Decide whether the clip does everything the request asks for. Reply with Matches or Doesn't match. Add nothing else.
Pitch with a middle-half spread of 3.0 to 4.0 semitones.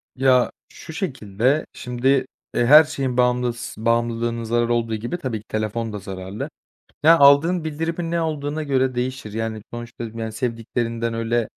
Matches